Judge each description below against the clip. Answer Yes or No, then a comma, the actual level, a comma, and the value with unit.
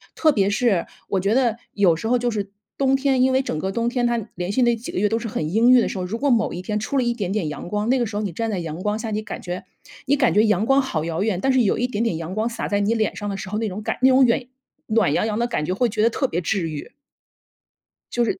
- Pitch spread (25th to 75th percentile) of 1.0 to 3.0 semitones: No, average, 3.8 semitones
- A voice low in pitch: No, high, 220 Hz